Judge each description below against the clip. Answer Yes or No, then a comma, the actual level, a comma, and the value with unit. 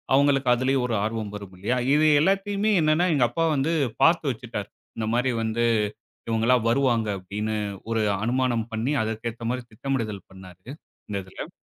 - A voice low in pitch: Yes, low, 120 Hz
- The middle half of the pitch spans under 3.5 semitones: No, average, 3.9 semitones